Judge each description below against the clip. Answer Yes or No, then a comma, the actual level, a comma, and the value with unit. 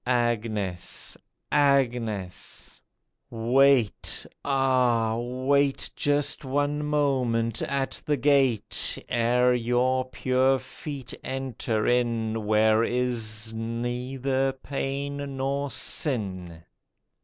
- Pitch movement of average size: Yes, average, 3.1 semitones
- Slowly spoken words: Yes, slow, 80 wpm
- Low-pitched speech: Yes, low, 125 Hz